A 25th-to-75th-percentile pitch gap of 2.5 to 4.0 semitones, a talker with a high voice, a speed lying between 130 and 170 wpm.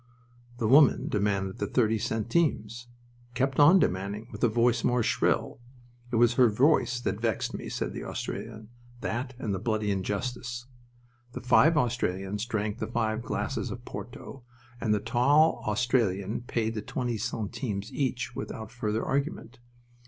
No: average, 2.8 semitones; low, 115 Hz; average, 150 wpm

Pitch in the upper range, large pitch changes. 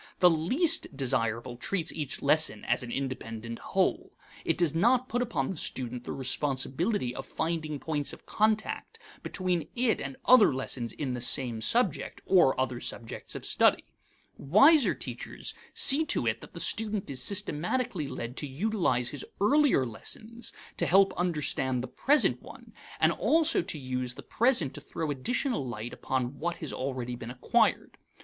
No: medium, 150 Hz; wide, 8.3 semitones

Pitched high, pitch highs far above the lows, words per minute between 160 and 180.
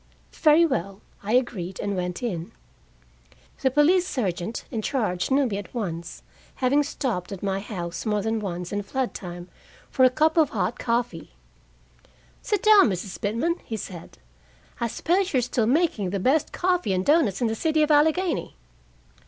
Yes: high, 230 Hz; wide, 7.4 semitones; average, 170 wpm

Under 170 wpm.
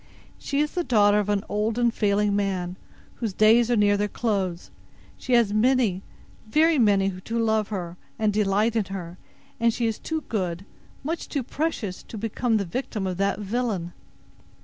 No: average, 175 wpm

